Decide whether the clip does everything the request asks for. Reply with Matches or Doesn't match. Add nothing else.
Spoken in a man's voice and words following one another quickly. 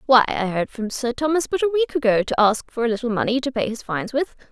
Doesn't match